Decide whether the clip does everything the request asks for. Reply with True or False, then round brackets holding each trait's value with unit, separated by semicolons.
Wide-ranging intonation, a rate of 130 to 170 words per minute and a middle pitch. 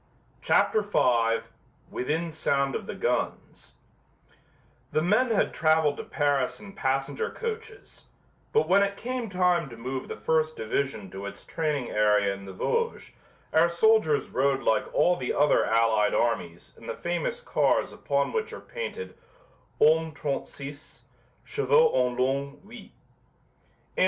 True (7.6 semitones; 140 wpm; 145 Hz)